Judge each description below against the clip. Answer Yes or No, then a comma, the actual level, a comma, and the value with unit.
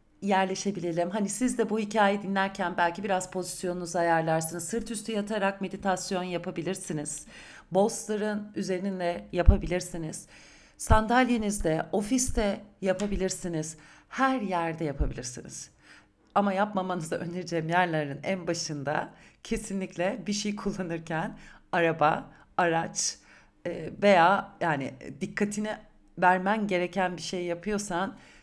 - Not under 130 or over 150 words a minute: No, slow, 95 wpm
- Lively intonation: No, average, 3.0 semitones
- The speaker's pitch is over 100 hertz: Yes, medium, 185 Hz